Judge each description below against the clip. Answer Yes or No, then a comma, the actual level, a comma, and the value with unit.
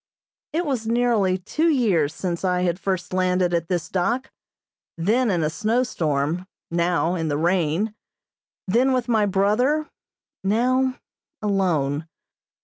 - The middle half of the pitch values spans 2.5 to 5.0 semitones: No, wide, 5.6 semitones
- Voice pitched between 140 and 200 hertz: Yes, high, 190 Hz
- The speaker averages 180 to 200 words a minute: No, slow, 135 wpm